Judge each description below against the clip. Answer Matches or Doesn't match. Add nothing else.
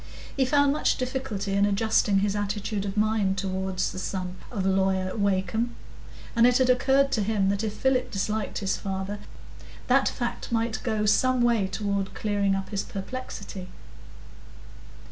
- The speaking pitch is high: Matches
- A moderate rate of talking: Matches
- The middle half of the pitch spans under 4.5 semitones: Matches